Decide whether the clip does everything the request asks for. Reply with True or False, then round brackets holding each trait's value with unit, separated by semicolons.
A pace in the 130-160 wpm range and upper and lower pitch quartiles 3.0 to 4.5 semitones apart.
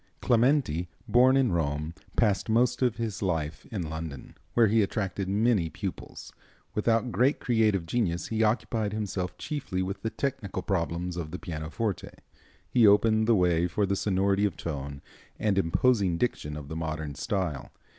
False (155 wpm; 5.3 semitones)